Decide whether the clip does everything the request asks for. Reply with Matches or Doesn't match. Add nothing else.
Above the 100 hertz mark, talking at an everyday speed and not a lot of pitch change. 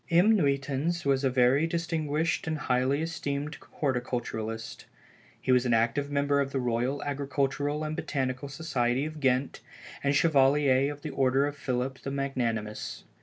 Matches